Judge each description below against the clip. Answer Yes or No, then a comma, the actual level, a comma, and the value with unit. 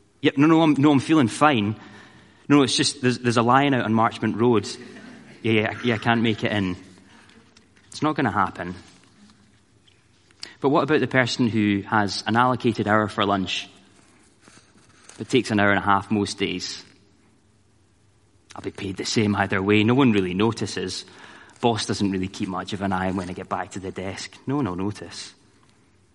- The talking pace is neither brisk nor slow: Yes, average, 195 wpm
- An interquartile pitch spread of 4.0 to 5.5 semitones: No, average, 3.0 semitones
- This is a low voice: Yes, low, 105 Hz